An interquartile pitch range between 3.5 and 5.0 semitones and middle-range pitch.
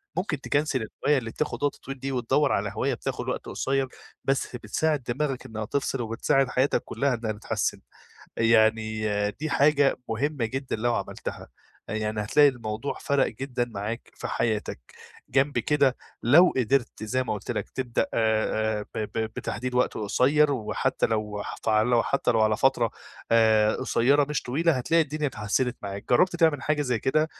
No: average, 4.4 semitones; low, 125 Hz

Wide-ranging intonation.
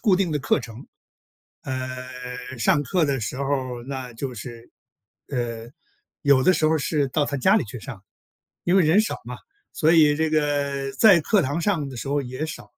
No: average, 3.7 semitones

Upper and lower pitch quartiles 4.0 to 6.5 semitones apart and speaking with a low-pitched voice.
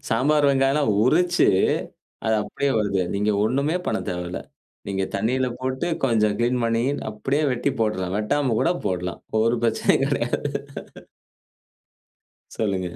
Yes: average, 4.7 semitones; low, 115 Hz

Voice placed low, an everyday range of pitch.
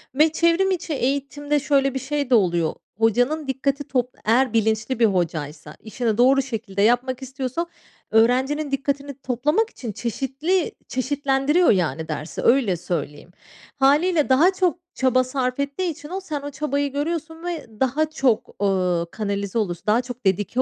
No: very high, 265 Hz; average, 4.7 semitones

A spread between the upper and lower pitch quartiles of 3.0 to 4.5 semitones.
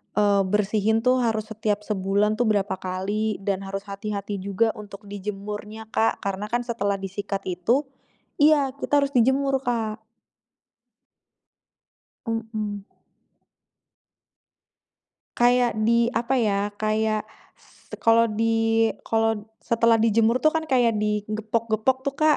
No: narrow, 2.4 semitones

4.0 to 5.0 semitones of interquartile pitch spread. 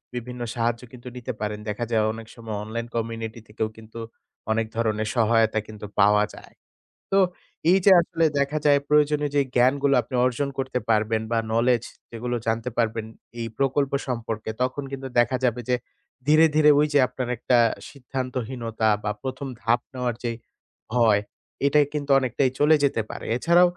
No: average, 3.3 semitones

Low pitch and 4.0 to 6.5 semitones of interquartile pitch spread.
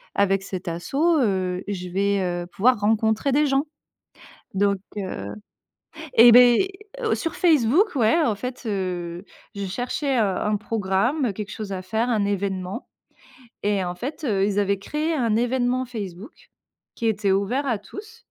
No: high, 210 Hz; average, 4.6 semitones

